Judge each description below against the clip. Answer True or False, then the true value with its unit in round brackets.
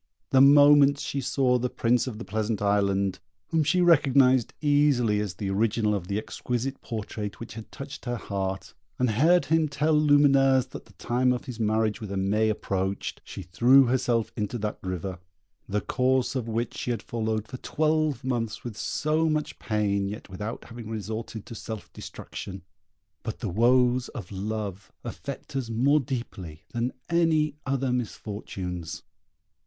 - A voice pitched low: True (115 Hz)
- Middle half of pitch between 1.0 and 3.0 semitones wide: False (4.4 semitones)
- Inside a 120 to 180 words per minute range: True (160 wpm)